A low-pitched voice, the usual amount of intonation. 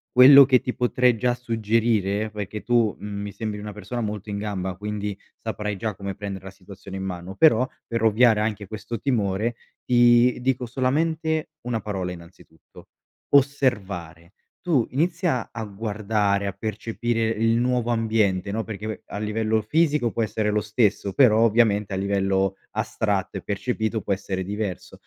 Yes: low, 110 Hz; average, 3.1 semitones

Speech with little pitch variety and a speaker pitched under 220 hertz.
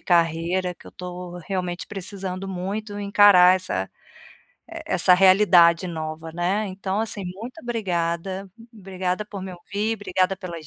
Yes: narrow, 2.3 semitones; medium, 185 Hz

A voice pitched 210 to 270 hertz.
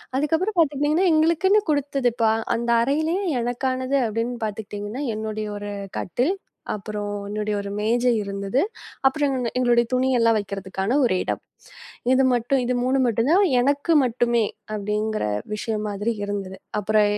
Yes: high, 235 Hz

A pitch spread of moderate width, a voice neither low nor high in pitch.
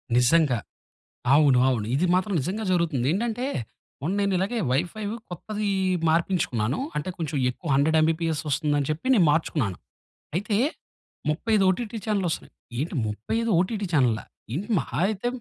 No: wide, 5.9 semitones; medium, 165 Hz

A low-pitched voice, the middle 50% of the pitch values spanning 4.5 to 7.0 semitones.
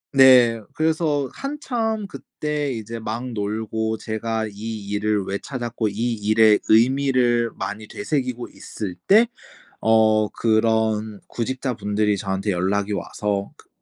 No: low, 110 Hz; average, 3.4 semitones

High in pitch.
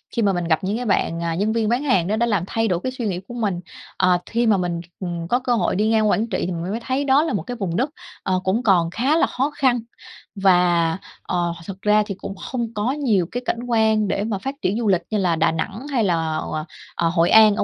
Yes: high, 205 Hz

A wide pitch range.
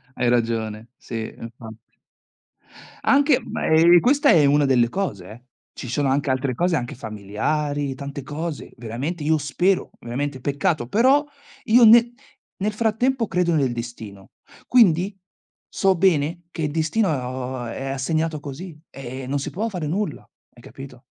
Yes: wide, 6.4 semitones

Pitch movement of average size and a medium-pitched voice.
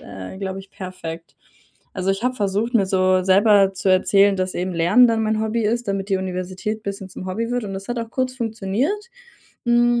No: average, 3.4 semitones; high, 200 Hz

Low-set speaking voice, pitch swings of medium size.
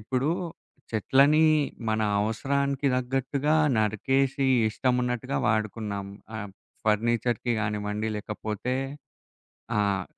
Yes: low, 115 Hz; average, 4.0 semitones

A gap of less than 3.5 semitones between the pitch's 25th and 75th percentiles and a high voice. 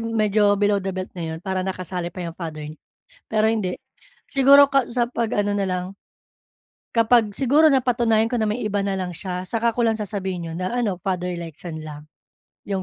No: average, 3.9 semitones; high, 205 Hz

